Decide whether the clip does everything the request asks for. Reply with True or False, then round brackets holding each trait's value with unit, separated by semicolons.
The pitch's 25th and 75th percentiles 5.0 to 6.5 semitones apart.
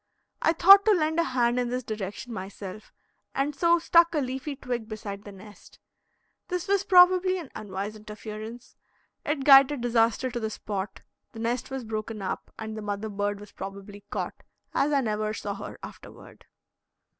True (5.3 semitones)